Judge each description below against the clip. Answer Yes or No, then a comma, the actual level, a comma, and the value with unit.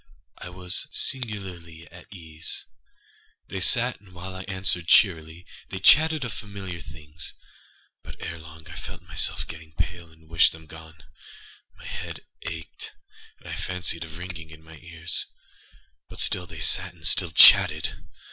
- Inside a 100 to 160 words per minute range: Yes, average, 155 wpm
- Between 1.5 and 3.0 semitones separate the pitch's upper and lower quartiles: Yes, narrow, 2.6 semitones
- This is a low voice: Yes, very low, 85 Hz